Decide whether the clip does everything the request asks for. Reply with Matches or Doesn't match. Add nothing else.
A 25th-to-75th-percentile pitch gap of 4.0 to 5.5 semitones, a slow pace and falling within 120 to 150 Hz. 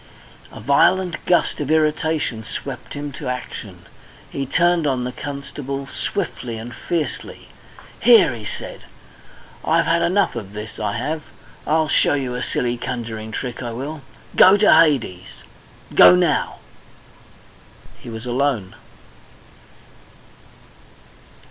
Matches